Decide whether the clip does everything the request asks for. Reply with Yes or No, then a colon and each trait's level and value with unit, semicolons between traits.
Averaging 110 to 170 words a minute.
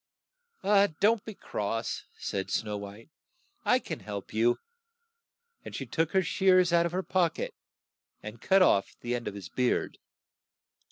Yes: average, 160 wpm